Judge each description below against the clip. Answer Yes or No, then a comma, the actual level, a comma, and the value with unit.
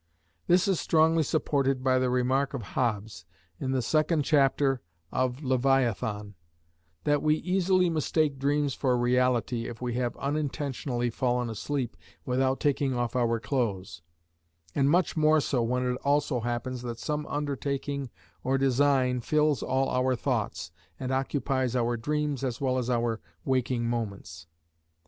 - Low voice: Yes, low, 130 Hz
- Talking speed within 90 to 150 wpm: Yes, average, 145 wpm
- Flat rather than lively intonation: No, average, 3.0 semitones